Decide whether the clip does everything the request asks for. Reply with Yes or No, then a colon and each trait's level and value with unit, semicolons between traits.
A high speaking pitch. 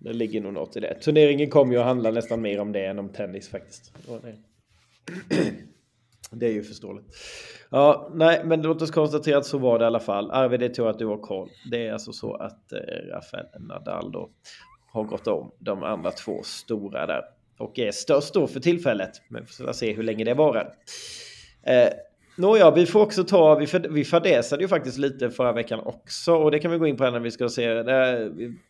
No: low, 130 Hz